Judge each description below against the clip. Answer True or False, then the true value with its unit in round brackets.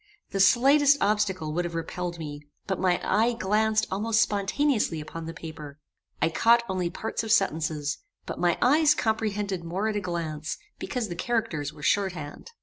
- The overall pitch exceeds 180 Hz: True (190 Hz)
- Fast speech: False (170 wpm)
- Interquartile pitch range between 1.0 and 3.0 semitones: False (5.1 semitones)